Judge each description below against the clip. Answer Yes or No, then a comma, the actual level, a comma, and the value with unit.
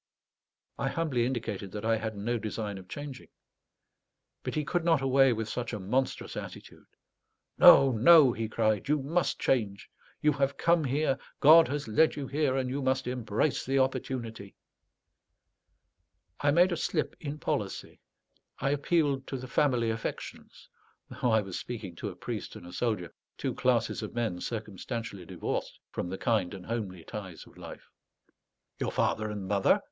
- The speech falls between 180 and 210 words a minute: No, average, 165 wpm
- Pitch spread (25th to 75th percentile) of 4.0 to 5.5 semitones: Yes, average, 4.6 semitones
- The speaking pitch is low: Yes, low, 120 Hz